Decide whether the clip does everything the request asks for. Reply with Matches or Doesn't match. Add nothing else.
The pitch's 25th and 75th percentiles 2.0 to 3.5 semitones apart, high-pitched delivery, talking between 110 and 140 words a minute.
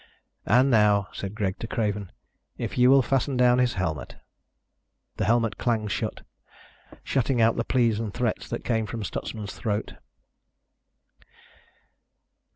Doesn't match